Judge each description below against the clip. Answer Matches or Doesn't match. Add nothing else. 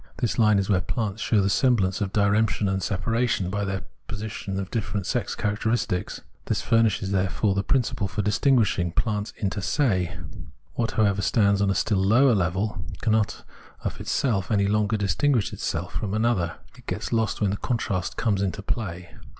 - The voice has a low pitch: Matches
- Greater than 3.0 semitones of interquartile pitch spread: Doesn't match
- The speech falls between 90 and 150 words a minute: Doesn't match